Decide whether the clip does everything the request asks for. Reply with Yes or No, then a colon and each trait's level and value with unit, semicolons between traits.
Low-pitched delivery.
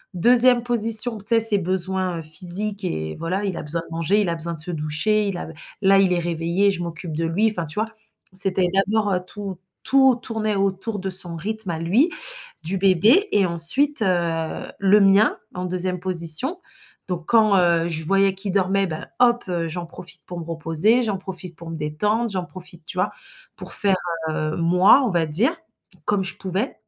No: medium, 185 Hz